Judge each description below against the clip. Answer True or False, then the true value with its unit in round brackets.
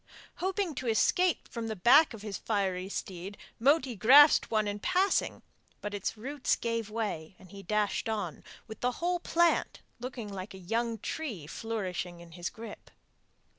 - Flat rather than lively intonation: False (4.8 semitones)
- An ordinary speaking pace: True (165 wpm)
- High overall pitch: True (220 Hz)